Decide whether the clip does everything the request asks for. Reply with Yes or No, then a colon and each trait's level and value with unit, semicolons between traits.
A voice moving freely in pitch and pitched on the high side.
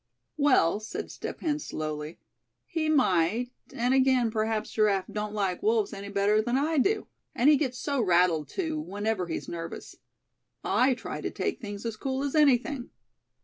Yes: wide, 5.9 semitones; high, 235 Hz